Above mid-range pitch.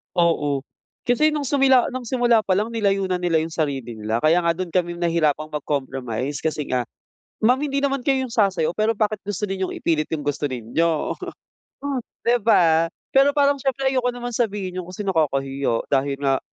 No: medium, 180 Hz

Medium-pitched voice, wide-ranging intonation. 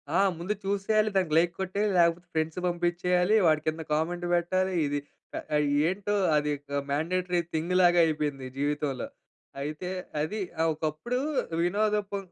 No: medium, 175 Hz; average, 3.3 semitones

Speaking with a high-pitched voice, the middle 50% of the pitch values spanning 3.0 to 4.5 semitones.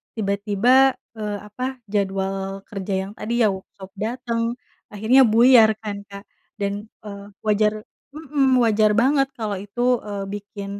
Yes: high, 215 Hz; average, 3.3 semitones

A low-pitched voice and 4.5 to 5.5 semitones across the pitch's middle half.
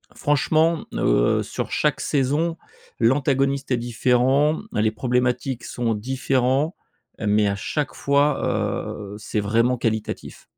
No: low, 125 Hz; average, 3.9 semitones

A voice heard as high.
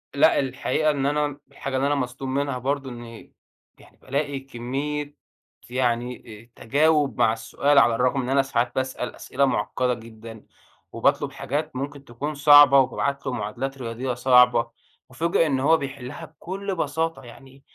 No: low, 135 Hz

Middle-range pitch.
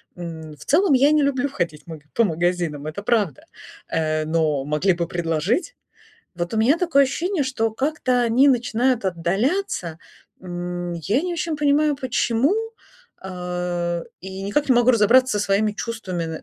No: high, 205 Hz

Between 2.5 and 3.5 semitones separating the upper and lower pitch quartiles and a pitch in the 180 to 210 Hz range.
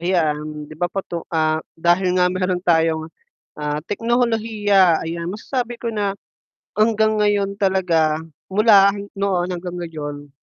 No: average, 4.1 semitones; medium, 185 Hz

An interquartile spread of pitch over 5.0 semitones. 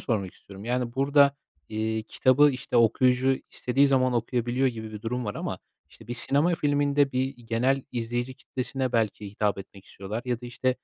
No: average, 2.9 semitones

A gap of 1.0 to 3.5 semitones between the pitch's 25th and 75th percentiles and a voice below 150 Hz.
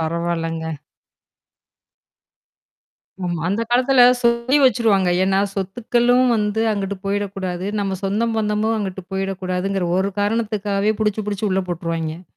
No: average, 3.0 semitones; high, 200 Hz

